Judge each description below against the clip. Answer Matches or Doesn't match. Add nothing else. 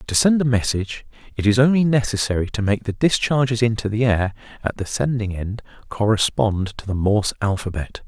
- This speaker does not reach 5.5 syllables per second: Doesn't match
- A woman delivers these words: Doesn't match